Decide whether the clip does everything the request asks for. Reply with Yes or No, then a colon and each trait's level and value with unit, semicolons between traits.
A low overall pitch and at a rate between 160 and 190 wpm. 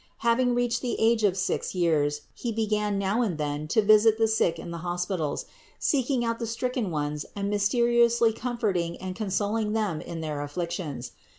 No: high, 205 Hz; average, 175 wpm